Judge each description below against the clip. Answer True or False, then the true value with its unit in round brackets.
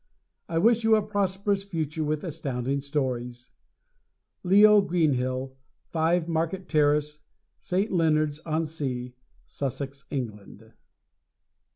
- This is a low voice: False (155 Hz)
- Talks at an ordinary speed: False (100 wpm)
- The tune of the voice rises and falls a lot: False (4.9 semitones)